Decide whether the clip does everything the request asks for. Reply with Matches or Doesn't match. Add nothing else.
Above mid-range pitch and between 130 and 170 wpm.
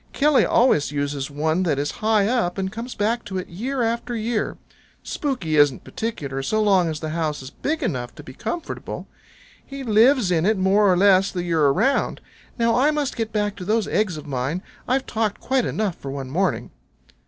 Doesn't match